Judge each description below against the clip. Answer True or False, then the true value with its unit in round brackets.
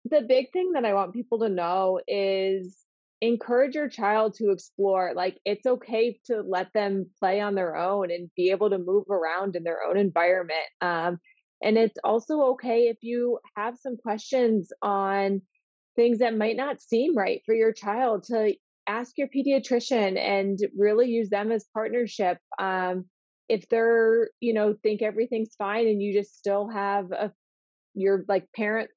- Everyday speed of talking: True (170 wpm)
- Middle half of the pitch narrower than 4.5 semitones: True (3.1 semitones)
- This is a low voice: False (210 Hz)